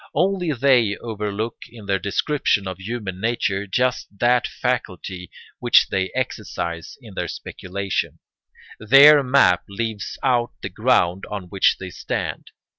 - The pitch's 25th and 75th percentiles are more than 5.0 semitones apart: No, average, 4.5 semitones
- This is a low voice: Yes, low, 105 Hz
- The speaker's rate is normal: No, slow, 130 wpm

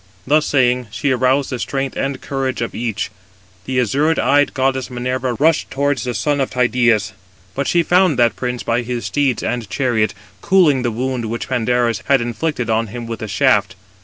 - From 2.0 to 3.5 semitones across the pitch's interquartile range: Yes, average, 2.7 semitones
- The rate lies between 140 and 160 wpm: No, average, 185 wpm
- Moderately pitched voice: No, low, 125 Hz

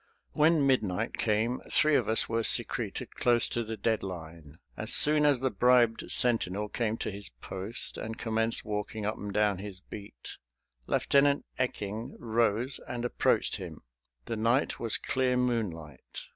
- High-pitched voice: No, low, 115 Hz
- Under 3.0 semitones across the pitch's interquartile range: No, average, 3.3 semitones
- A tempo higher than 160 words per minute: No, average, 155 wpm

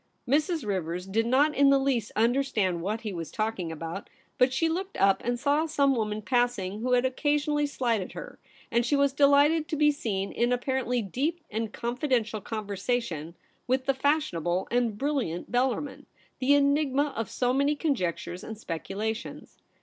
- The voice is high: Yes, high, 245 Hz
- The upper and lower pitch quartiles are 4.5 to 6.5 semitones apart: Yes, average, 5.2 semitones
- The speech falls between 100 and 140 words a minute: No, average, 170 wpm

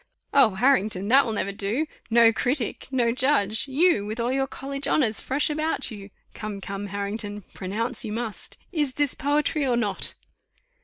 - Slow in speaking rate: No, average, 165 wpm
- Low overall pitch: No, high, 235 Hz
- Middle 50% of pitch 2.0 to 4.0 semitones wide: No, average, 5.0 semitones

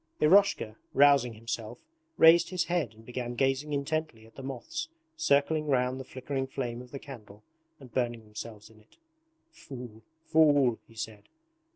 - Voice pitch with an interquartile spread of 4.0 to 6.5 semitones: Yes, average, 4.3 semitones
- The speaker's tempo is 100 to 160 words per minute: Yes, average, 155 wpm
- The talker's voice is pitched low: Yes, low, 130 Hz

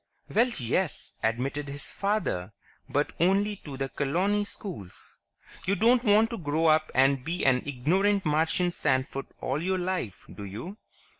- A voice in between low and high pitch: Yes, medium, 160 Hz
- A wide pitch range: Yes, wide, 6.5 semitones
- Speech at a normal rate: Yes, average, 150 wpm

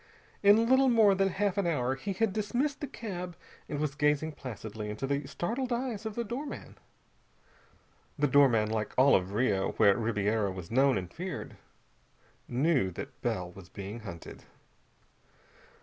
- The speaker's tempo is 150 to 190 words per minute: Yes, average, 155 wpm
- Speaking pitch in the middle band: Yes, medium, 145 Hz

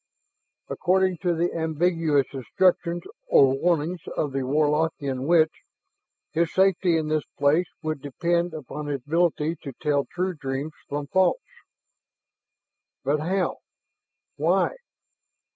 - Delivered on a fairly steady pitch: No, average, 3.2 semitones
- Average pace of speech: No, slow, 115 wpm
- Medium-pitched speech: Yes, medium, 160 Hz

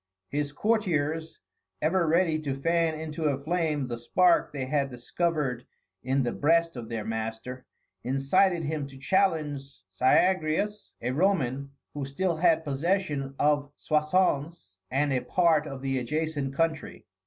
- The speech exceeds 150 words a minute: No, average, 140 wpm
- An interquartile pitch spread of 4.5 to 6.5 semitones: No, average, 3.5 semitones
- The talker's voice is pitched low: No, medium, 150 Hz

